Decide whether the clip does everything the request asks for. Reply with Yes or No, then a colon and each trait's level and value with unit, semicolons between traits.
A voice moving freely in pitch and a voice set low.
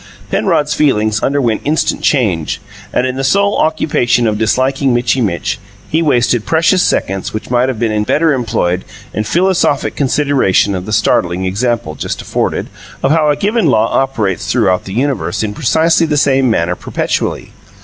Yes: wide, 5.7 semitones; low, 125 Hz